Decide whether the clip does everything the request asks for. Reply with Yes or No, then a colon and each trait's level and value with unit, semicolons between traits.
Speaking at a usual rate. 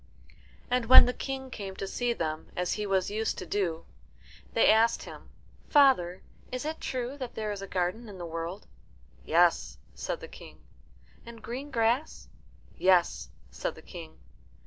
Yes: average, 165 wpm